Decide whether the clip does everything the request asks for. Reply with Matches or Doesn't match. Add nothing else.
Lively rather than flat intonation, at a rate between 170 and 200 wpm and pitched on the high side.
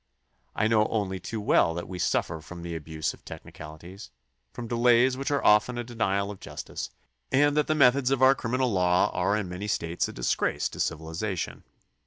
Doesn't match